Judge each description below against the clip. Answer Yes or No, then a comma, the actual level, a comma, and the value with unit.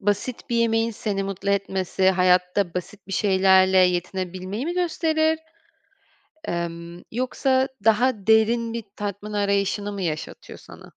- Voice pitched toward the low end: No, high, 200 Hz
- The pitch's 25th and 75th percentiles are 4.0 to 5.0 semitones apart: No, average, 3.4 semitones